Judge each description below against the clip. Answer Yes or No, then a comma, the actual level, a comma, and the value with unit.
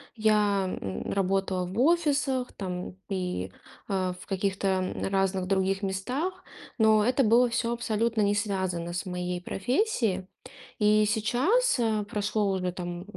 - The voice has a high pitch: Yes, high, 200 Hz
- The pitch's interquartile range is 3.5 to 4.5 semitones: Yes, average, 3.8 semitones